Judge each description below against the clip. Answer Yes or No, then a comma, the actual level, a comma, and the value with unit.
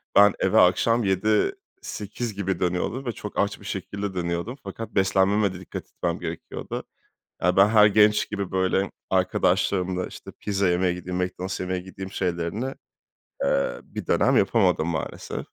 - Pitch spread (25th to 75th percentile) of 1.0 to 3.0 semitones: Yes, narrow, 2.4 semitones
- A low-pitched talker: Yes, very low, 95 Hz